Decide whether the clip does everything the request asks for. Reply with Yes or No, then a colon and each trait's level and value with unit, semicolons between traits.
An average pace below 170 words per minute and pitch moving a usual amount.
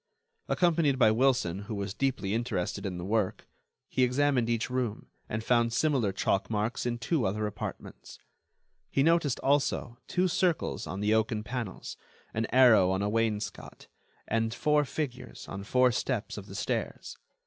Yes: average, 160 wpm; average, 4.1 semitones